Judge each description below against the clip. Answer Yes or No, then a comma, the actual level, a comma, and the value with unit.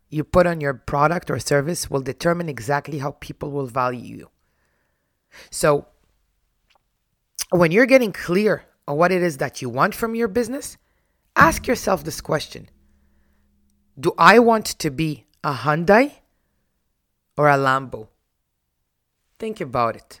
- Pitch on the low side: No, medium, 145 Hz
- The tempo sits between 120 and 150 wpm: Yes, average, 140 wpm